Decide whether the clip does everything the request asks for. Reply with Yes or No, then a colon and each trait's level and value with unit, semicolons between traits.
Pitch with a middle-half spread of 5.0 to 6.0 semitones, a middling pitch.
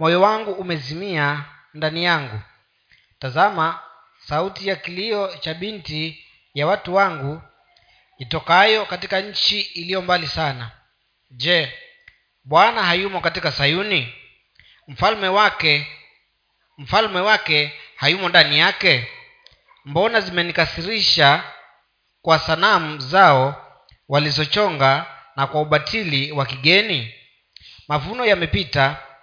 Yes: average, 5.3 semitones; medium, 165 Hz